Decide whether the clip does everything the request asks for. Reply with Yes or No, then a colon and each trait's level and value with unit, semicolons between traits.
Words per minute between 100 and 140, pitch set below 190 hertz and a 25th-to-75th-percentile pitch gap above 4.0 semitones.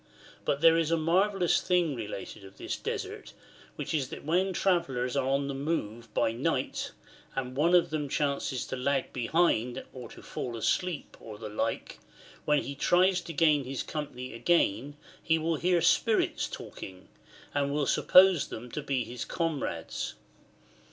No: average, 165 wpm; medium, 140 Hz; average, 5.0 semitones